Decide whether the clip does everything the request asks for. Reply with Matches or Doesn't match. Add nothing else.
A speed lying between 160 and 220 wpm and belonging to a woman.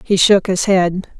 Matches